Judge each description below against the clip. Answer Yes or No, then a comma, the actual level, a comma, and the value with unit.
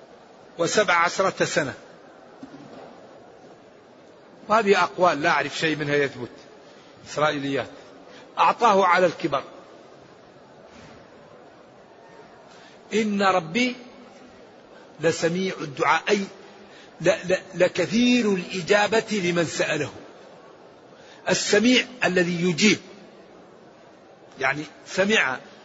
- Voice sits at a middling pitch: Yes, medium, 180 Hz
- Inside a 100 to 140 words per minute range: No, slow, 65 wpm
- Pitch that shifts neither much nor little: Yes, average, 4.4 semitones